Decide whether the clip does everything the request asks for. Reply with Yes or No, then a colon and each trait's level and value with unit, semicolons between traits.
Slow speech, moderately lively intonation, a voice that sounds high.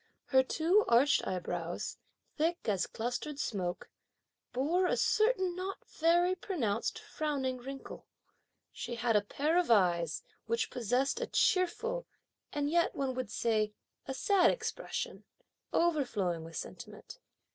No: slow, 125 wpm; wide, 7.7 semitones; very high, 270 Hz